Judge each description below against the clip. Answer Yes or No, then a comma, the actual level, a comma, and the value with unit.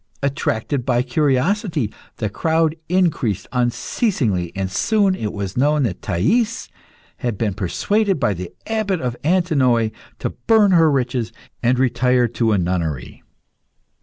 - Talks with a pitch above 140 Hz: No, low, 125 Hz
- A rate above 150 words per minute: No, slow, 135 wpm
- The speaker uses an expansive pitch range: Yes, wide, 7.4 semitones